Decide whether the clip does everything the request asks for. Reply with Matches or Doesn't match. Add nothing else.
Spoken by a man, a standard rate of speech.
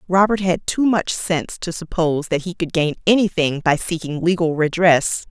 Doesn't match